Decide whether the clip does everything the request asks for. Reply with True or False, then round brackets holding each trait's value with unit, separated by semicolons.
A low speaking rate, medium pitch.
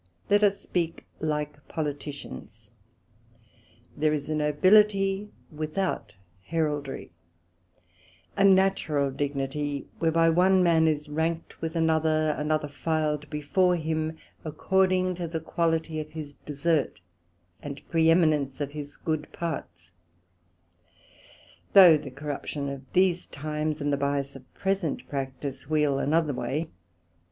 True (115 wpm; 155 Hz)